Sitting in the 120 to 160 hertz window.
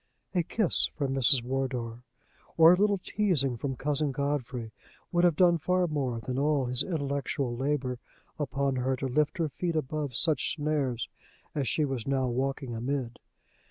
Yes: medium, 140 Hz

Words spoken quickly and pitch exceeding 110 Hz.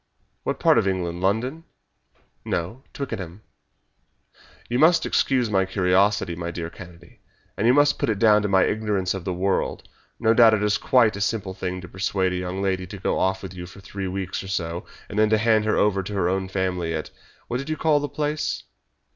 No: fast, 210 wpm; very low, 95 Hz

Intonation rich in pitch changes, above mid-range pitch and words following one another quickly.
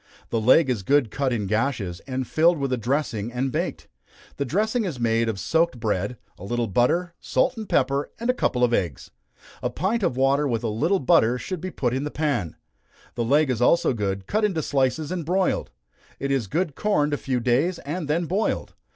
No: wide, 5.8 semitones; low, 135 Hz; fast, 210 wpm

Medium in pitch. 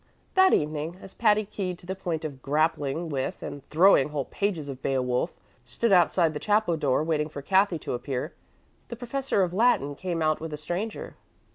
Yes: medium, 160 Hz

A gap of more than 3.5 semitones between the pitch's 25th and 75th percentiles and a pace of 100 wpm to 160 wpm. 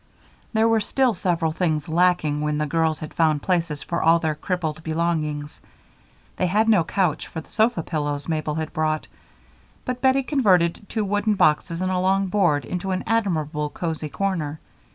No: average, 3.9 semitones; average, 175 wpm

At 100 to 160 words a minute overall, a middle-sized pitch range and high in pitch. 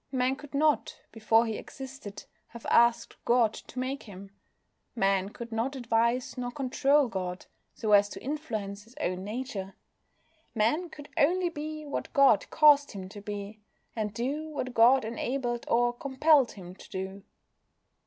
Yes: average, 155 wpm; average, 4.9 semitones; high, 240 Hz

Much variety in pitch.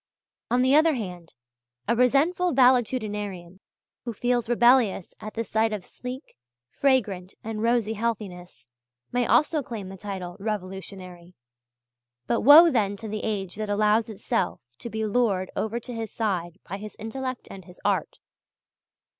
No: average, 4.0 semitones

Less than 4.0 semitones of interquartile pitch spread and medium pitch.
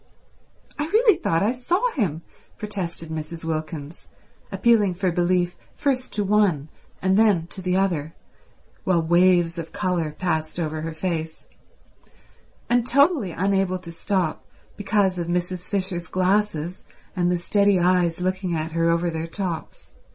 Yes: average, 3.2 semitones; medium, 180 Hz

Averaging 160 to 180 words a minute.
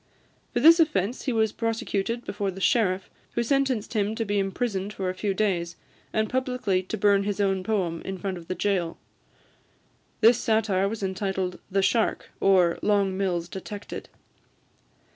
Yes: average, 165 wpm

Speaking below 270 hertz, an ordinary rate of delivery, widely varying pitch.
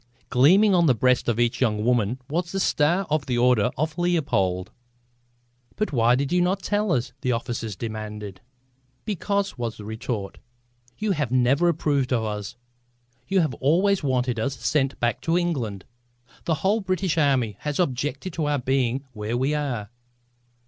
Yes: low, 135 Hz; average, 165 wpm; wide, 6.3 semitones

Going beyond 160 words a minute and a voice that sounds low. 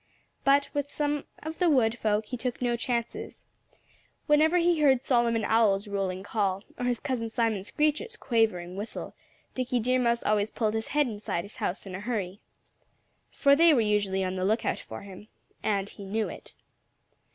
No: average, 175 wpm; high, 230 Hz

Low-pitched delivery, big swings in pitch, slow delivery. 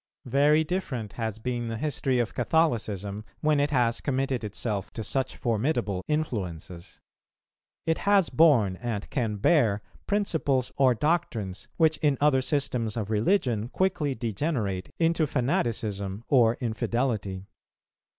Yes: low, 120 Hz; wide, 5.7 semitones; slow, 125 wpm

